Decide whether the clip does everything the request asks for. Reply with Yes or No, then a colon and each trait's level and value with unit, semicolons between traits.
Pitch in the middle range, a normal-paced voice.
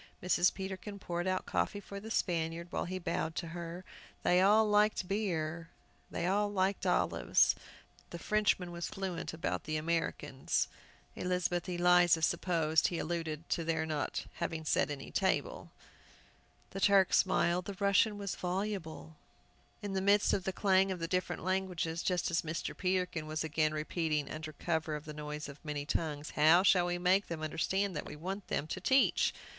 Yes: medium, 175 Hz; average, 170 wpm